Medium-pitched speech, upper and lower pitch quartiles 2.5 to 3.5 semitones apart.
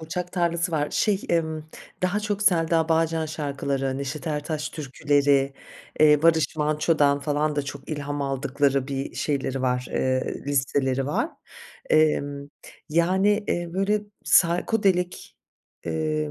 Yes: medium, 150 Hz; average, 3.1 semitones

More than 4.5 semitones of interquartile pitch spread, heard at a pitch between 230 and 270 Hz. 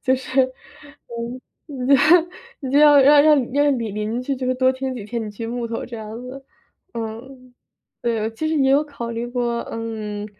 No: average, 3.0 semitones; very high, 250 Hz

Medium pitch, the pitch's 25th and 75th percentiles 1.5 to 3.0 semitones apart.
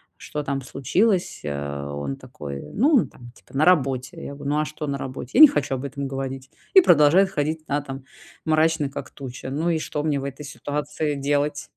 Yes: medium, 145 Hz; narrow, 2.6 semitones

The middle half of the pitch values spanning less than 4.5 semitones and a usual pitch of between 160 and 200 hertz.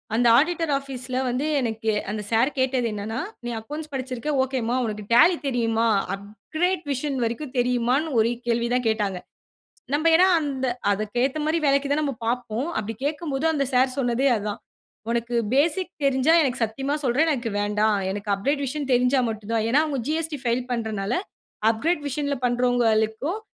No: average, 4.1 semitones; very high, 250 Hz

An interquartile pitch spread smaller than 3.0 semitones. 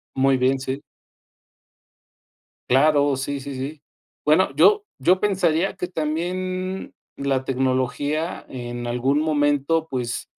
No: average, 3.8 semitones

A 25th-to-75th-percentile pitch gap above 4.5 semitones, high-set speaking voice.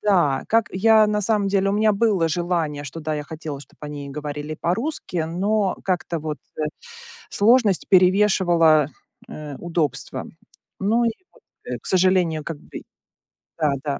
No: average, 5.0 semitones; medium, 175 Hz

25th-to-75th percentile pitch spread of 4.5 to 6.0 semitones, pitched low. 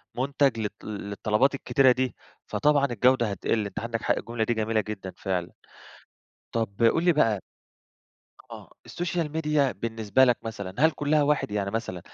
Yes: average, 4.8 semitones; low, 115 Hz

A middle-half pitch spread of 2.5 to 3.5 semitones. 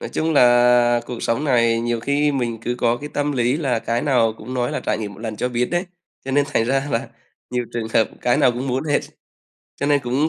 Yes: average, 3.1 semitones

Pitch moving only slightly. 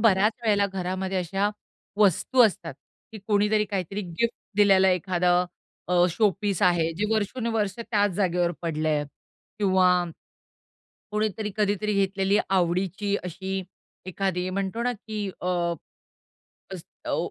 Yes: narrow, 2.3 semitones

